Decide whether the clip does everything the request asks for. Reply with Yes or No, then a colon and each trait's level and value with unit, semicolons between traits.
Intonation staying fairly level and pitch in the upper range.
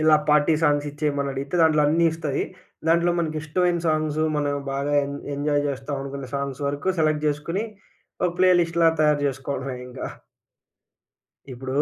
No: narrow, 2.0 semitones; medium, 150 Hz